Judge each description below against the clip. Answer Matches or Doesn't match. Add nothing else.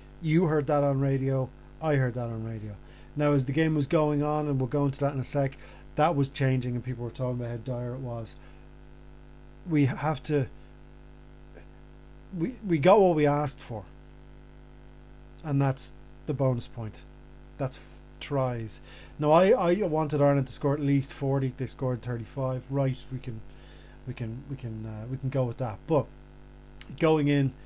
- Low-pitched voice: Matches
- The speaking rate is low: Doesn't match